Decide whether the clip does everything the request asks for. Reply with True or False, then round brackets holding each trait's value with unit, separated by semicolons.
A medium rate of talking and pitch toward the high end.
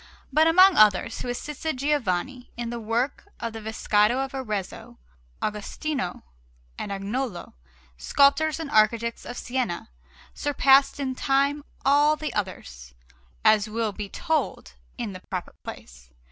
False (130 wpm; 240 Hz)